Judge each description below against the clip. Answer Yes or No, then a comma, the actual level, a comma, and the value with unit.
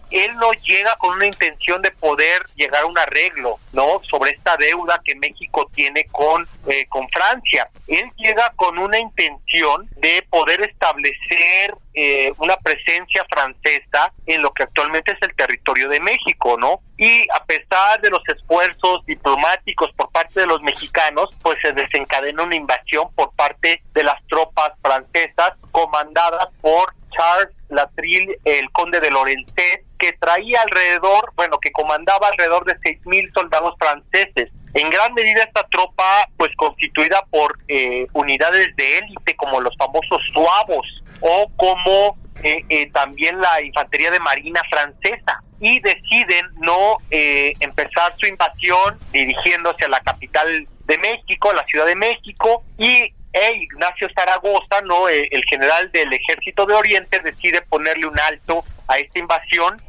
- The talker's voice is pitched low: No, medium, 175 Hz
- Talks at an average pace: Yes, average, 150 wpm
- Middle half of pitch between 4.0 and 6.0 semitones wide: Yes, average, 4.7 semitones